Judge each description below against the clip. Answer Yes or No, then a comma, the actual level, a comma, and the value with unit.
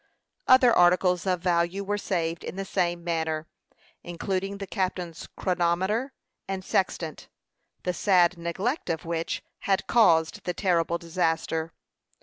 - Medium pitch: Yes, medium, 180 Hz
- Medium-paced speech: No, slow, 130 wpm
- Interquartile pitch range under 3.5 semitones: Yes, narrow, 2.4 semitones